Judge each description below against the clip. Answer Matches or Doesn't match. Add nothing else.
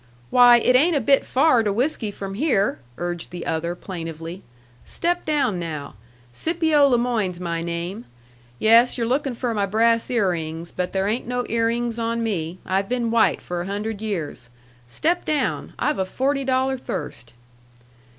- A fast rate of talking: Doesn't match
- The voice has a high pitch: Matches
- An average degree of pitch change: Doesn't match